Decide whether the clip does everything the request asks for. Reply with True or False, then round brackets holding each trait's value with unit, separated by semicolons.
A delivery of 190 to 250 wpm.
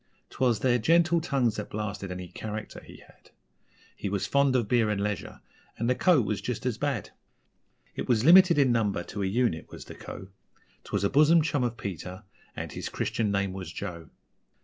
True (195 wpm)